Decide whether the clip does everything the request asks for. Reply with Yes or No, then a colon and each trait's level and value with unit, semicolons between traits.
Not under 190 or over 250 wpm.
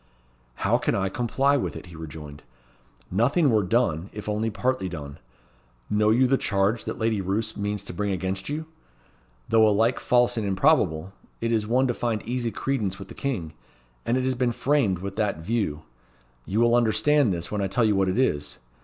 Yes: average, 195 wpm